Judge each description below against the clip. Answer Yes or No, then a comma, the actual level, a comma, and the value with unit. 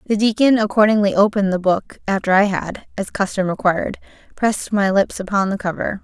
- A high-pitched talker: Yes, high, 200 Hz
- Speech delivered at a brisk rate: No, average, 180 wpm